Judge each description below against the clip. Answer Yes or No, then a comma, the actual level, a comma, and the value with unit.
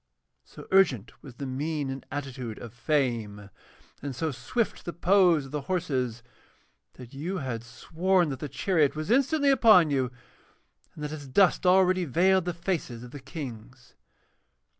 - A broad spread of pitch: Yes, wide, 5.9 semitones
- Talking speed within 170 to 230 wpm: No, average, 160 wpm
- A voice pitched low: No, medium, 145 Hz